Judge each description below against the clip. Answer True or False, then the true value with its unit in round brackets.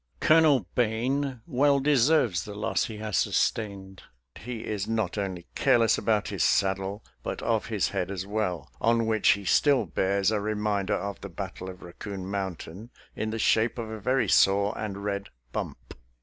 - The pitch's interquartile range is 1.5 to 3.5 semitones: True (2.9 semitones)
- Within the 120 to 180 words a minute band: True (170 wpm)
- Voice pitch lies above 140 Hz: False (105 Hz)